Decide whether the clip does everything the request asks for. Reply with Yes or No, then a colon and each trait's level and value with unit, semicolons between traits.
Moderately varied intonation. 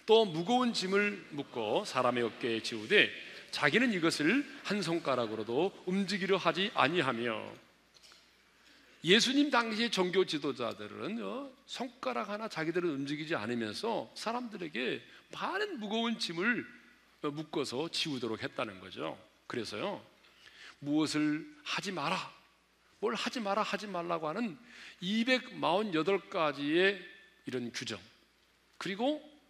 No: wide, 7.5 semitones